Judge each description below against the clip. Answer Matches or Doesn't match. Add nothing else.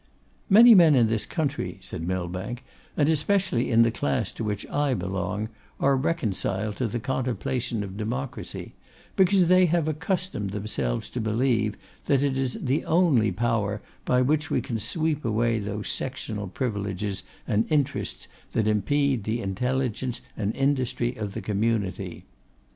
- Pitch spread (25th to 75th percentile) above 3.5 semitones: Matches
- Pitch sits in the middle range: Doesn't match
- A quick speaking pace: Doesn't match